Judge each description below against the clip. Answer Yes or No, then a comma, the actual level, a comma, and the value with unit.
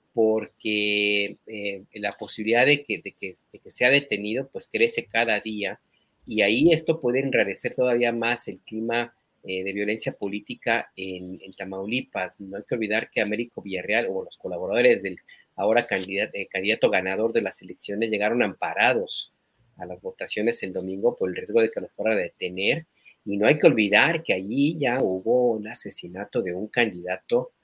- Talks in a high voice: No, low, 115 Hz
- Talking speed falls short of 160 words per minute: No, average, 180 wpm